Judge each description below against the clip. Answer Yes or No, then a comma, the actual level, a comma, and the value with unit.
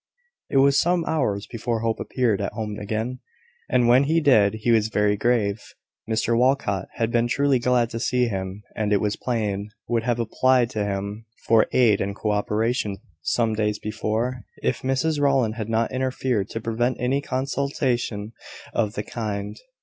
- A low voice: Yes, low, 115 Hz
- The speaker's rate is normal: Yes, average, 170 wpm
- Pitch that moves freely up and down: No, average, 3.3 semitones